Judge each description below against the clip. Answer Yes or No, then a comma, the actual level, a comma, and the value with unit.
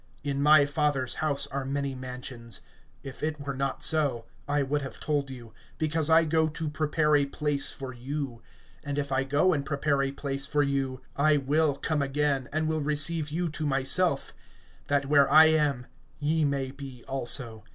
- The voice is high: No, medium, 140 Hz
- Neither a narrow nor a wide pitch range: No, narrow, 1.9 semitones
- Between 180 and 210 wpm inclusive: Yes, average, 185 wpm